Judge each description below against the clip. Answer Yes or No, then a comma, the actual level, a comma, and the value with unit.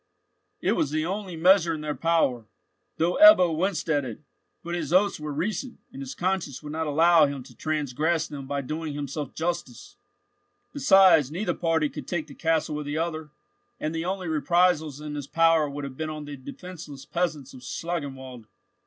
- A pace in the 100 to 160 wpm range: No, average, 185 wpm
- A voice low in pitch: No, medium, 155 Hz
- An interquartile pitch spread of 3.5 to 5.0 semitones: No, average, 3.1 semitones